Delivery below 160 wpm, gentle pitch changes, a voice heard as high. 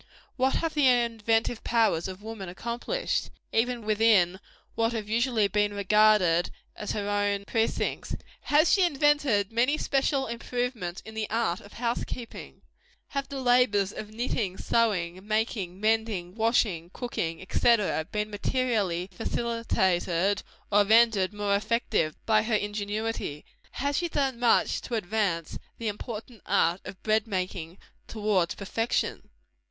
No: slow, 135 wpm; average, 3.0 semitones; high, 215 Hz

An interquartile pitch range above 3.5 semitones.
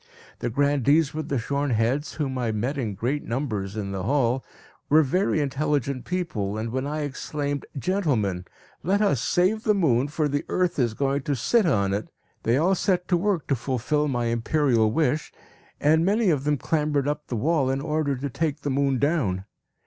Yes: average, 4.3 semitones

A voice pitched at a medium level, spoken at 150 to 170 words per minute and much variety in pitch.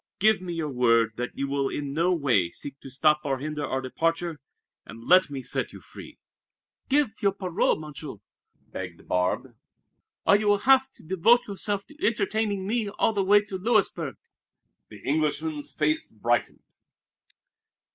Yes: medium, 160 Hz; average, 160 wpm; wide, 6.6 semitones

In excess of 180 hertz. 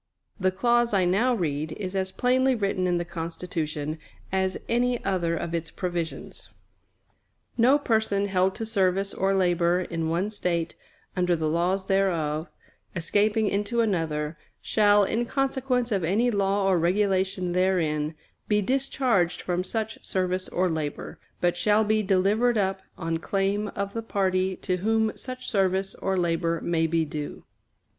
Yes: high, 190 Hz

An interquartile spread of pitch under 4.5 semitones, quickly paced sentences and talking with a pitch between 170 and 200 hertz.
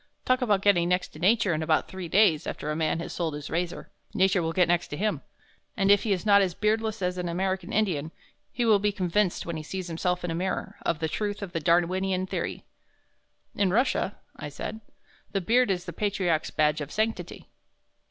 Yes: average, 3.4 semitones; fast, 210 wpm; medium, 185 Hz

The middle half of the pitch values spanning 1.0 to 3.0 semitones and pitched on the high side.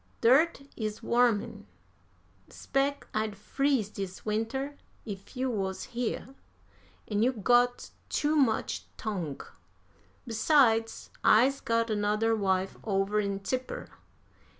No: average, 3.5 semitones; high, 225 Hz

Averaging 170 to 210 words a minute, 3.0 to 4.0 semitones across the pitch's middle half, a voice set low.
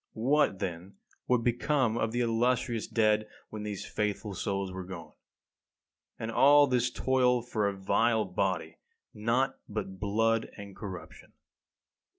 No: slow, 135 wpm; average, 3.5 semitones; low, 110 Hz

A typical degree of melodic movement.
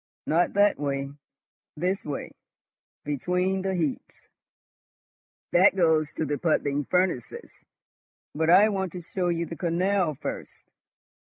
Yes: average, 3.8 semitones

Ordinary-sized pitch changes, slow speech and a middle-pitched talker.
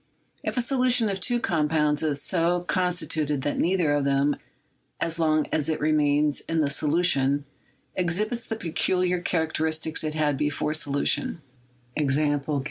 No: average, 3.3 semitones; average, 150 wpm; medium, 155 Hz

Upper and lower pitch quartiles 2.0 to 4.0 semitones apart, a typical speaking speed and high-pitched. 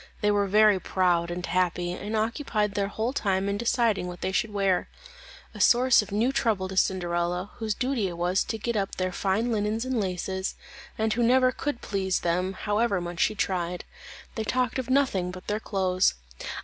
Yes: average, 3.3 semitones; average, 190 wpm; high, 200 Hz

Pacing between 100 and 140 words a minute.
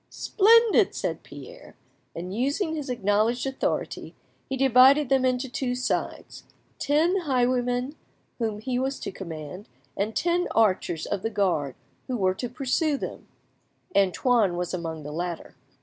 Yes: slow, 135 wpm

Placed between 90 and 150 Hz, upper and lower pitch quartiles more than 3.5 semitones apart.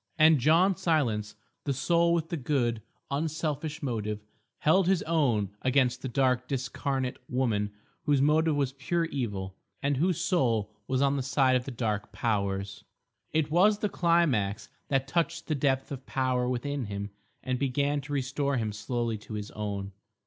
Yes: low, 135 Hz; average, 4.7 semitones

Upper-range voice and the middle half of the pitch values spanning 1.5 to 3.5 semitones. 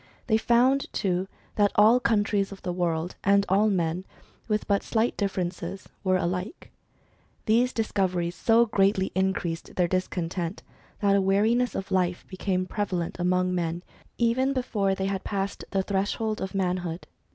Yes: high, 195 Hz; average, 2.7 semitones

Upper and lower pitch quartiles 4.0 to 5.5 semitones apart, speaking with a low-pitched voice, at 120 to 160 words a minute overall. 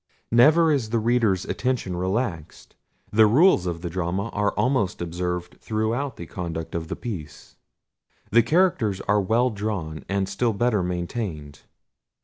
Yes: average, 5.1 semitones; low, 105 Hz; average, 140 wpm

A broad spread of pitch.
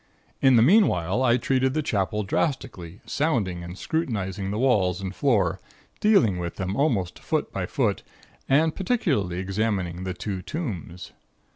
Yes: wide, 6.6 semitones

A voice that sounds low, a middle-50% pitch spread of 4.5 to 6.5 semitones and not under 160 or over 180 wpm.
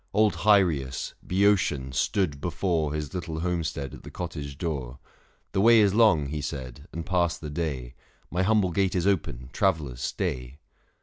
Yes: very low, 80 Hz; average, 5.3 semitones; average, 165 wpm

